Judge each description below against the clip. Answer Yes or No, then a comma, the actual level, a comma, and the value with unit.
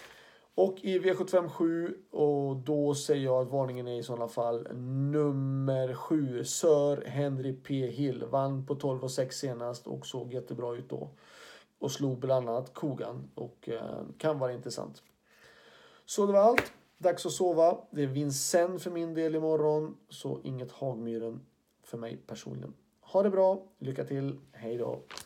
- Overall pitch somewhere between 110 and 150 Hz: Yes, medium, 140 Hz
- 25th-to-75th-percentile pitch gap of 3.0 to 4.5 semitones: Yes, average, 3.9 semitones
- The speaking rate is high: No, average, 160 wpm